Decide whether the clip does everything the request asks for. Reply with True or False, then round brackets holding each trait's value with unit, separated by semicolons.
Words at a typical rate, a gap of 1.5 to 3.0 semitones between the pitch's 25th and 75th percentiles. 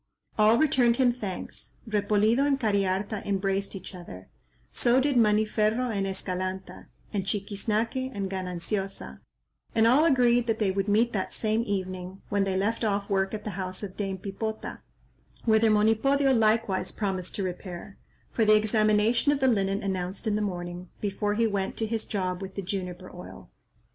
True (165 wpm; 2.7 semitones)